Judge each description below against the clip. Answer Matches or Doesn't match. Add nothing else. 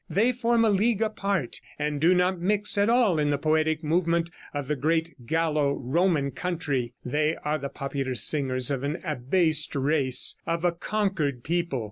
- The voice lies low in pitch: Doesn't match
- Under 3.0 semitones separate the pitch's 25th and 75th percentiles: Doesn't match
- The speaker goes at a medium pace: Matches